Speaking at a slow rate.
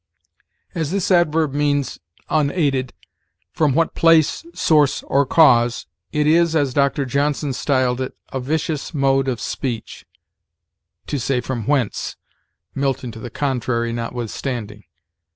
Yes: slow, 125 wpm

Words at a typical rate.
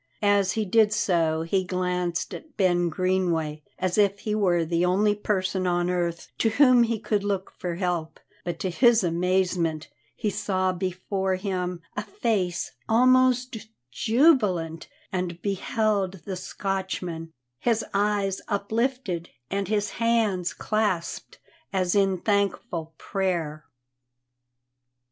No: slow, 125 wpm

